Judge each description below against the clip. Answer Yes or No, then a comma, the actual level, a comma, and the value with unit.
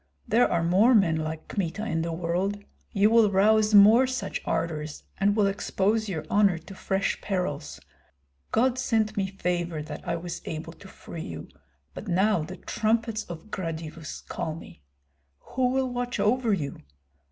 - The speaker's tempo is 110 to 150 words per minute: No, average, 165 wpm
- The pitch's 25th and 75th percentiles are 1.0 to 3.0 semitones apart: No, average, 4.6 semitones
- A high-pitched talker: Yes, high, 195 Hz